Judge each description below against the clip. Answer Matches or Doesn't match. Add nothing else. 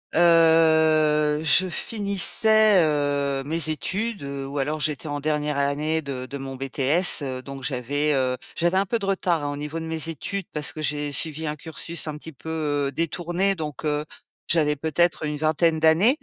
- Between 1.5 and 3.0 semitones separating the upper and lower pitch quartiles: Matches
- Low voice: Doesn't match